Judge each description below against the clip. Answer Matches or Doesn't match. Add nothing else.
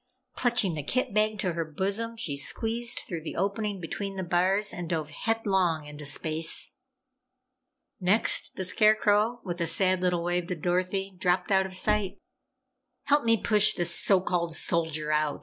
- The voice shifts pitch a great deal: Doesn't match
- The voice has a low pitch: Doesn't match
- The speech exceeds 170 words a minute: Doesn't match